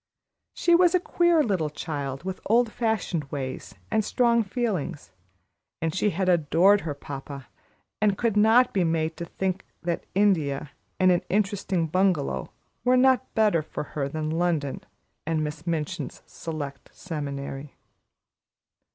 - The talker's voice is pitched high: No, medium, 175 Hz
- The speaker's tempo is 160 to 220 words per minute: No, average, 140 wpm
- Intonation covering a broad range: Yes, wide, 5.8 semitones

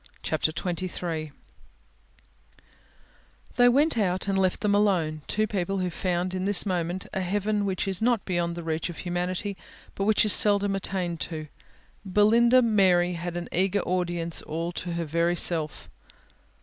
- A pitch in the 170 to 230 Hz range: Yes, medium, 185 Hz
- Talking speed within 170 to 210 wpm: No, average, 155 wpm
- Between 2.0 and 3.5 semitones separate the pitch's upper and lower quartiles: Yes, average, 2.8 semitones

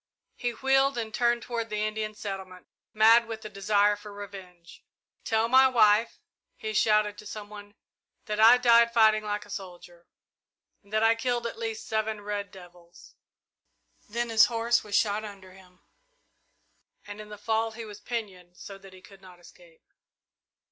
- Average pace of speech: Yes, average, 170 wpm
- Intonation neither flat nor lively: No, narrow, 2.2 semitones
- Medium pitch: No, high, 215 Hz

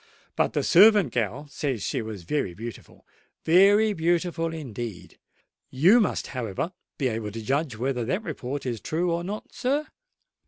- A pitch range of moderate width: No, wide, 7.2 semitones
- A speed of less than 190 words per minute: Yes, average, 150 wpm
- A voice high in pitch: No, medium, 145 Hz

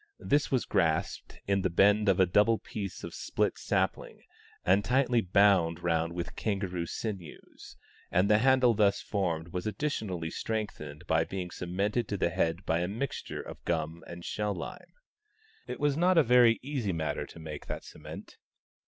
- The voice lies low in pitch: Yes, low, 100 Hz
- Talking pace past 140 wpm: Yes, average, 170 wpm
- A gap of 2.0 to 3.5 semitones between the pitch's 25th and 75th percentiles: No, average, 4.5 semitones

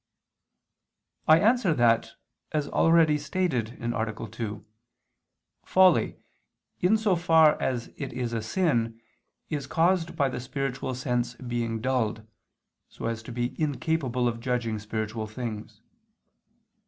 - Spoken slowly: Yes, slow, 120 wpm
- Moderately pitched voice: No, low, 125 Hz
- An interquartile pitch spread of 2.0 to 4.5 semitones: No, wide, 5.5 semitones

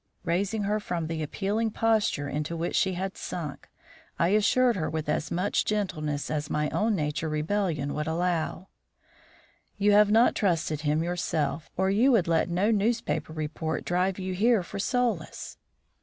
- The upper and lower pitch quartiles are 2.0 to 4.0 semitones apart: No, average, 4.8 semitones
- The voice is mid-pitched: Yes, medium, 180 Hz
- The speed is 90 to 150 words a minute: No, average, 160 wpm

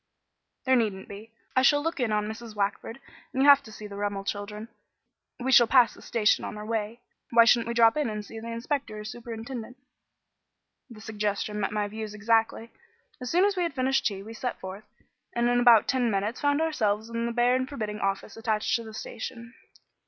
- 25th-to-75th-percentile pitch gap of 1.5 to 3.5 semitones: Yes, average, 2.7 semitones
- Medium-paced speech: No, fast, 210 wpm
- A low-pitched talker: No, high, 225 Hz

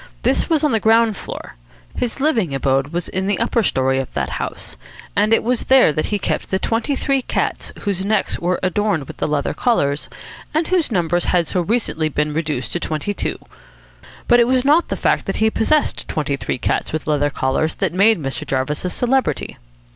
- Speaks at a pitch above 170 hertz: Yes, high, 190 Hz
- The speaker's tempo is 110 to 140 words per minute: No, average, 200 wpm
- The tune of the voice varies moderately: No, wide, 7.5 semitones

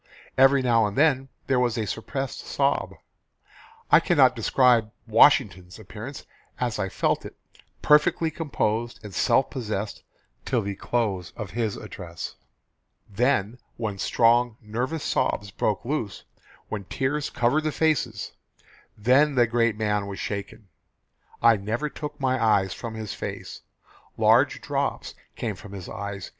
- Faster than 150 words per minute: No, average, 140 wpm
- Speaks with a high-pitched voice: No, low, 115 Hz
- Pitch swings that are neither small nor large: Yes, average, 4.2 semitones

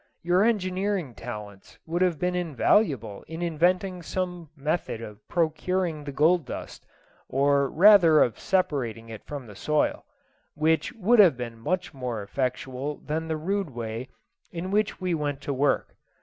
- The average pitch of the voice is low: No, medium, 155 Hz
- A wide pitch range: Yes, wide, 5.8 semitones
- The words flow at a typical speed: Yes, average, 150 wpm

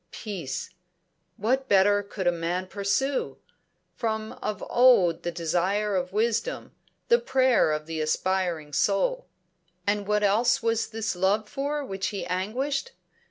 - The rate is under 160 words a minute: Yes, slow, 135 wpm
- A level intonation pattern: No, average, 4.4 semitones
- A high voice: Yes, high, 205 Hz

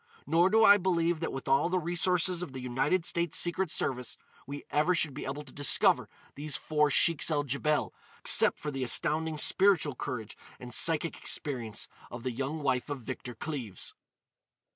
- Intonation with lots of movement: No, average, 4.2 semitones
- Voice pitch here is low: No, medium, 150 Hz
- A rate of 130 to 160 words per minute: No, average, 175 wpm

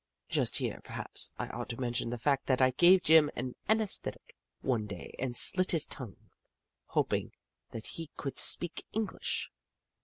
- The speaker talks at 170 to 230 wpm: No, average, 160 wpm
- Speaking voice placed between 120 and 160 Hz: Yes, low, 135 Hz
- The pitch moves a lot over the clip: Yes, wide, 6.1 semitones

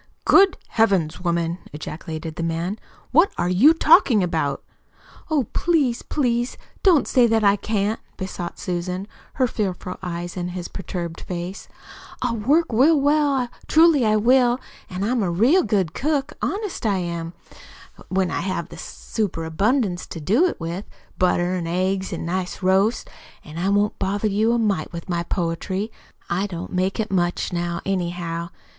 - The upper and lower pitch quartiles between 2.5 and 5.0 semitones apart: No, wide, 5.4 semitones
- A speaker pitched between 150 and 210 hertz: Yes, high, 190 Hz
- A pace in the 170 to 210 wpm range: No, average, 160 wpm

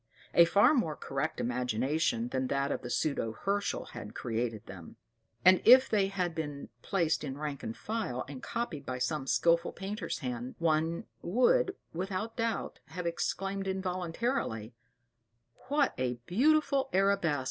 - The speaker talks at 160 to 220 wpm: No, average, 145 wpm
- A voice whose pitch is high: No, medium, 170 Hz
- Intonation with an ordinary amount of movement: No, wide, 7.2 semitones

